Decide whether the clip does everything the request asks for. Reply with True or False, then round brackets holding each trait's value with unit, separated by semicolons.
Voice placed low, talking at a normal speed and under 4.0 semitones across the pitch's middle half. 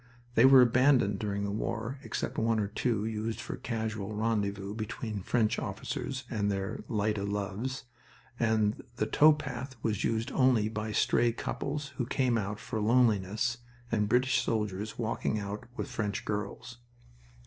True (110 Hz; 155 wpm; 2.7 semitones)